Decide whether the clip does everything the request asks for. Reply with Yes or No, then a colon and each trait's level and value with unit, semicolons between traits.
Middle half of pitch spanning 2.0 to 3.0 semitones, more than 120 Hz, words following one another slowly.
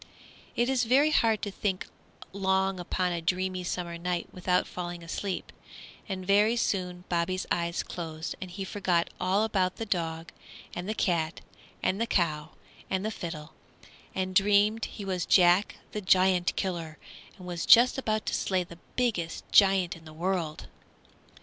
No: narrow, 2.6 semitones; medium, 185 Hz; average, 160 wpm